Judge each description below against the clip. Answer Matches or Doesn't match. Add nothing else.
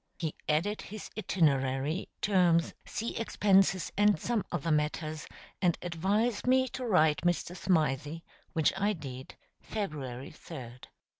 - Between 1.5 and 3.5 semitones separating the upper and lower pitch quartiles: Doesn't match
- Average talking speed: Doesn't match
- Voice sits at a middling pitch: Matches